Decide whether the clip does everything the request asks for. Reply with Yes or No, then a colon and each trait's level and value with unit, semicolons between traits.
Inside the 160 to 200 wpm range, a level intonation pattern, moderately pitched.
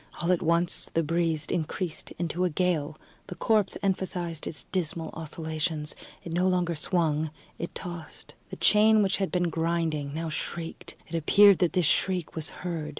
Yes: average, 165 wpm; narrow, 2.2 semitones; medium, 170 Hz